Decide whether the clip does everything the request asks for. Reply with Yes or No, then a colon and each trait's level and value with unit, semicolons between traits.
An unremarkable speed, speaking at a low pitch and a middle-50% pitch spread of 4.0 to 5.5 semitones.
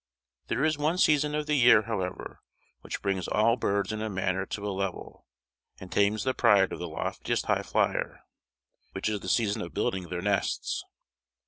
No: average, 180 wpm; low, 105 Hz; average, 3.6 semitones